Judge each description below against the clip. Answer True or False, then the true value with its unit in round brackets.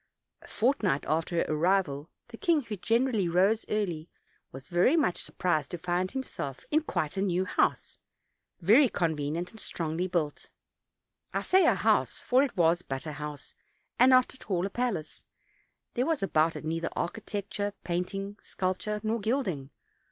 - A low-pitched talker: False (185 Hz)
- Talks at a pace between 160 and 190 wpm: True (165 wpm)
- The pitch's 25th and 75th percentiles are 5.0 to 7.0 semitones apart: True (5.5 semitones)